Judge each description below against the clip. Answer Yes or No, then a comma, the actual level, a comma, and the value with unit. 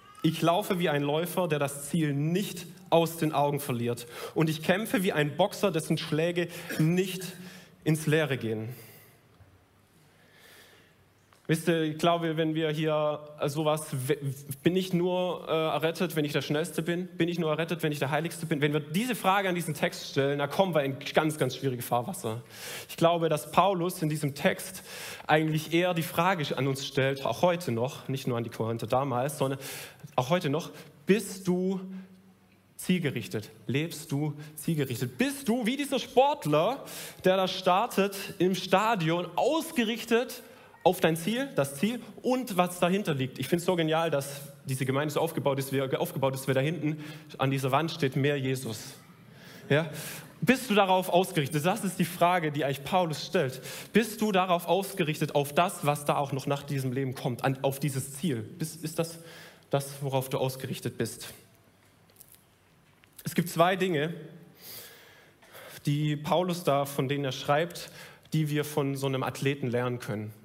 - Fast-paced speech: No, average, 170 wpm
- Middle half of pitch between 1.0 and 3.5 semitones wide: No, average, 4.3 semitones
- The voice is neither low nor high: Yes, medium, 155 Hz